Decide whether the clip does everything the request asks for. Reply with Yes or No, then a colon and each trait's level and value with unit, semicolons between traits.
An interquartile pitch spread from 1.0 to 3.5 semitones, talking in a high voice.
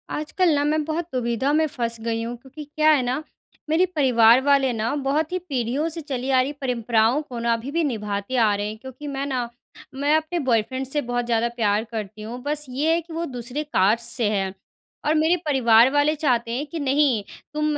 No: average, 4.3 semitones; very high, 260 Hz